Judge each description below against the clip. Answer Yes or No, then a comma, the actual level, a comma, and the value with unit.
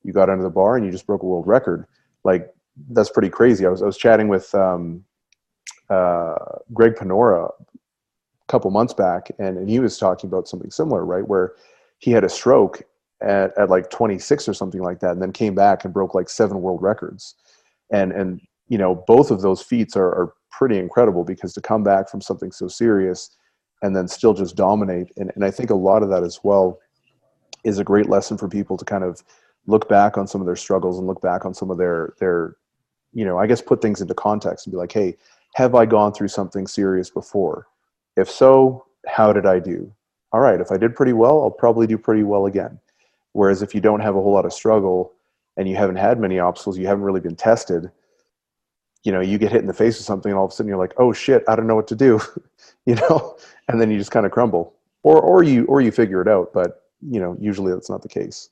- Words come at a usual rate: No, fast, 235 wpm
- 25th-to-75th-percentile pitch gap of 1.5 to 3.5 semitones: Yes, average, 2.7 semitones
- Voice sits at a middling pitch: No, low, 100 Hz